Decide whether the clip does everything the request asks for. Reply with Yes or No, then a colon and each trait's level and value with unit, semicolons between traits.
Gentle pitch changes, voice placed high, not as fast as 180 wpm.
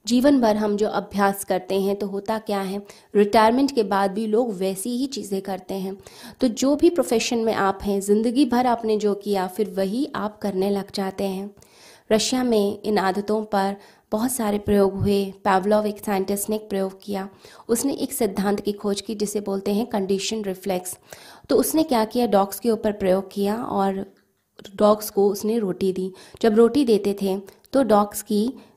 No: narrow, 2.3 semitones; high, 205 Hz; average, 185 wpm